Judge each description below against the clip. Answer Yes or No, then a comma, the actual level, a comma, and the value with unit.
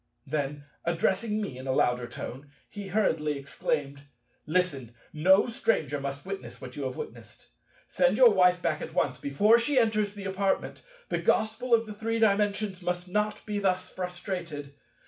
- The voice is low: No, medium, 185 Hz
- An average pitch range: No, wide, 6.3 semitones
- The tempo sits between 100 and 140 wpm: No, average, 160 wpm